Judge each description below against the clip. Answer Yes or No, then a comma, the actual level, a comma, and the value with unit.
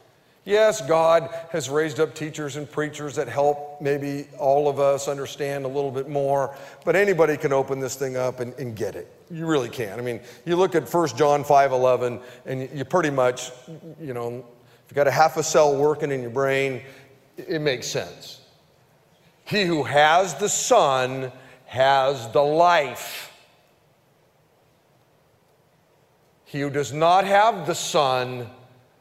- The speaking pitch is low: No, medium, 145 Hz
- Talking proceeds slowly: No, average, 160 wpm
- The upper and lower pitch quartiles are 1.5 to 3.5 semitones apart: Yes, average, 3.0 semitones